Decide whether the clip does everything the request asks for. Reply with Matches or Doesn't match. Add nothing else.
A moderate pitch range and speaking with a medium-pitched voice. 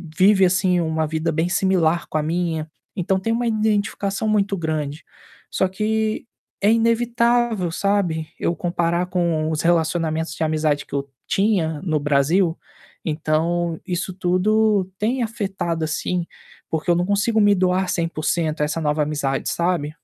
Matches